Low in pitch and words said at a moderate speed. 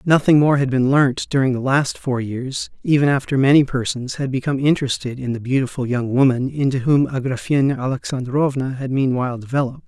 Yes: low, 130 Hz; average, 175 wpm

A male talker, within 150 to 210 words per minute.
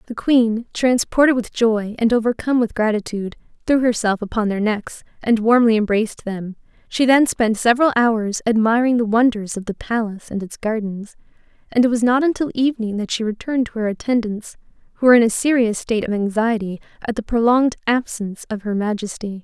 No: female; average, 180 wpm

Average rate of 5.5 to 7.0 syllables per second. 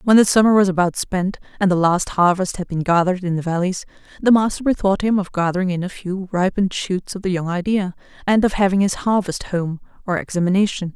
Yes: 6.0 syllables/s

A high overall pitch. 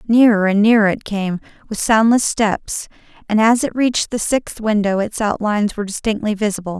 Yes: high, 215 Hz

